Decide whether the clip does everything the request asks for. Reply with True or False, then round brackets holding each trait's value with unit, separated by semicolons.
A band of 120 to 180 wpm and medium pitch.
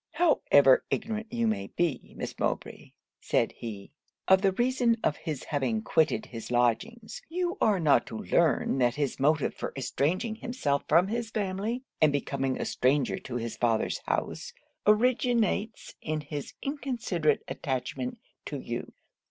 True (145 wpm; 175 Hz)